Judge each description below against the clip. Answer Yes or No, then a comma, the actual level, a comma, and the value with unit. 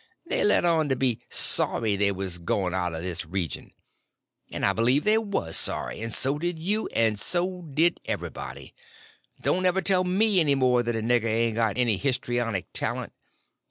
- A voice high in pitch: No, low, 120 Hz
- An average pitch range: No, wide, 9.0 semitones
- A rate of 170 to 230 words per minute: Yes, average, 180 wpm